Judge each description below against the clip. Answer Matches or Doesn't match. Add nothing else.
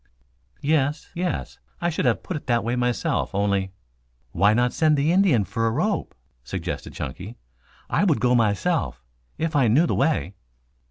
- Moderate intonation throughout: Doesn't match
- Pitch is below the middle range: Matches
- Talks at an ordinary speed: Matches